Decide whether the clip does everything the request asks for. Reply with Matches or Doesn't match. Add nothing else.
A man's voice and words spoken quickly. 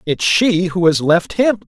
Doesn't match